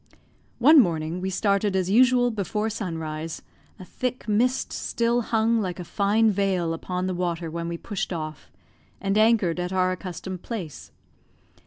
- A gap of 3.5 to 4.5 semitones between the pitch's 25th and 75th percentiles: Yes, average, 4.1 semitones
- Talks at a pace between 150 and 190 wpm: Yes, average, 155 wpm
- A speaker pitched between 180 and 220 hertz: Yes, high, 190 Hz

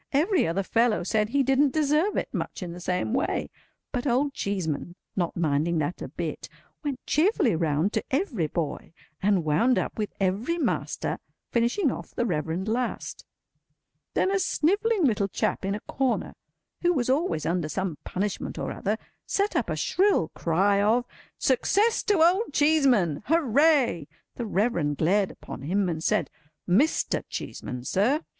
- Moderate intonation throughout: No, wide, 8.7 semitones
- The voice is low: No, high, 220 Hz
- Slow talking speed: No, average, 155 wpm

